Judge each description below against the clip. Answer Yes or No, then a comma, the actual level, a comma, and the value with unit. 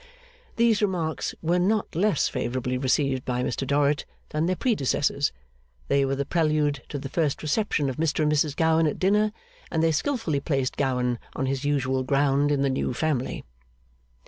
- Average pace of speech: Yes, average, 170 wpm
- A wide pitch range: No, average, 3.3 semitones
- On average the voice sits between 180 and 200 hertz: No, medium, 145 Hz